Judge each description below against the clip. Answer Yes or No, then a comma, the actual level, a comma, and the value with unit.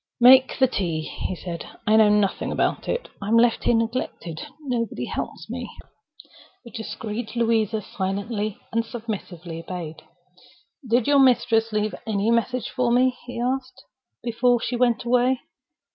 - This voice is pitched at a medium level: No, high, 230 Hz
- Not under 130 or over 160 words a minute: Yes, average, 145 wpm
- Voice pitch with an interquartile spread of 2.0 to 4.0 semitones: Yes, average, 2.9 semitones